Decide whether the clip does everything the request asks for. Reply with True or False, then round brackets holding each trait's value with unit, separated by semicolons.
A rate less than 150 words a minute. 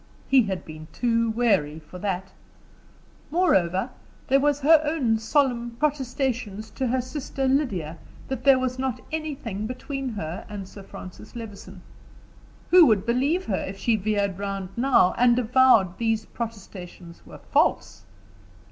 True (140 wpm)